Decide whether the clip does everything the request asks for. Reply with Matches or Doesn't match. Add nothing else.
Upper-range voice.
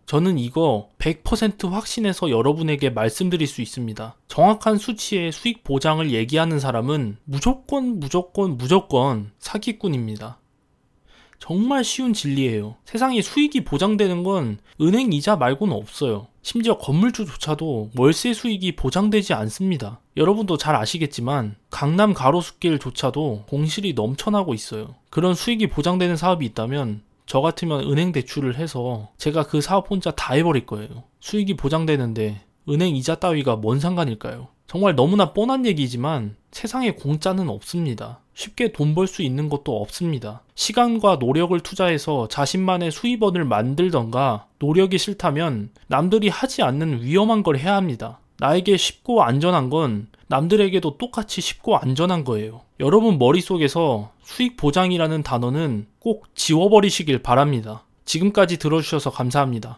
Doesn't match